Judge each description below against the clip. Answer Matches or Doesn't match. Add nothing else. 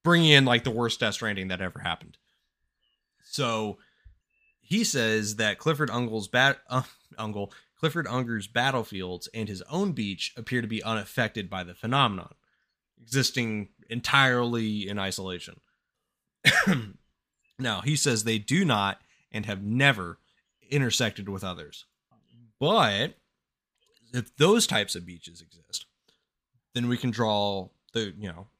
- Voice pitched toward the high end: Doesn't match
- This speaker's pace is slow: Matches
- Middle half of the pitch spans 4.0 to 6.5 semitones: Matches